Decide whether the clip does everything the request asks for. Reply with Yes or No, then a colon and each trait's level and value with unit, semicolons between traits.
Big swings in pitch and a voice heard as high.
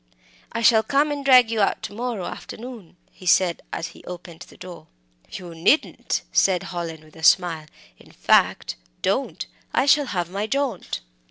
Yes: wide, 6.0 semitones; high, 195 Hz